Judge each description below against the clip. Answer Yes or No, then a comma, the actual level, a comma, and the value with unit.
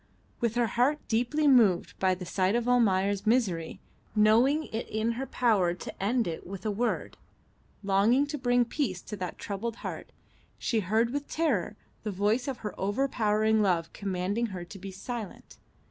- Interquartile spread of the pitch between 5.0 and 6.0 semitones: No, average, 3.9 semitones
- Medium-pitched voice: No, high, 215 Hz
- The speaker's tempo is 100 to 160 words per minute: No, average, 170 wpm